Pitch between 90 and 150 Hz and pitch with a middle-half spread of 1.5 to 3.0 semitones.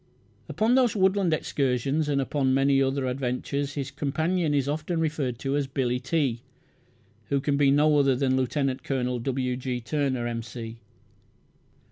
Yes: low, 135 Hz; narrow, 2.6 semitones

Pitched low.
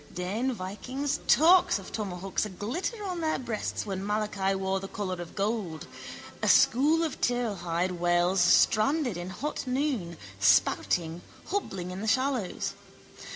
No: high, 205 Hz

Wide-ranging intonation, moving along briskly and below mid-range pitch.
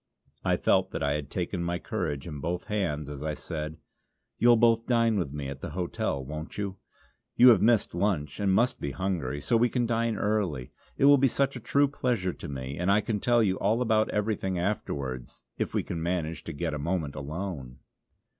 Yes: wide, 6.9 semitones; fast, 210 wpm; very low, 90 Hz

